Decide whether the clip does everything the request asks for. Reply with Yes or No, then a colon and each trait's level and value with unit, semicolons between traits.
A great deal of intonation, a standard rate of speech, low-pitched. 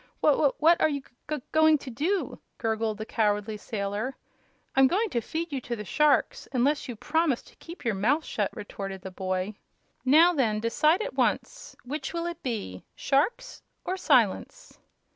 No: wide, 6.8 semitones; average, 180 wpm; very high, 270 Hz